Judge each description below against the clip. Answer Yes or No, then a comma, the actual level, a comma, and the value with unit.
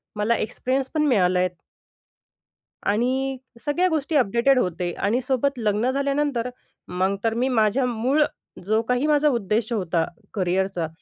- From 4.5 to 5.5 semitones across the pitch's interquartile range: Yes, average, 5.1 semitones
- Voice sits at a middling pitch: No, high, 235 Hz